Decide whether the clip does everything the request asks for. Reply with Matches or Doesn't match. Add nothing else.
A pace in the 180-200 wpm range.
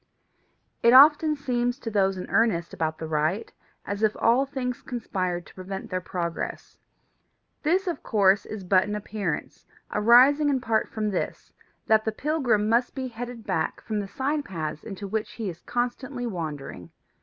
Doesn't match